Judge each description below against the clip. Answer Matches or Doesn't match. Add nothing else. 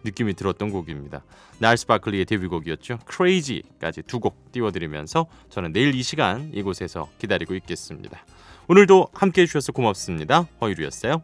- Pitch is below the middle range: Matches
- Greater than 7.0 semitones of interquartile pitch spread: Matches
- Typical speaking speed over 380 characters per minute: Matches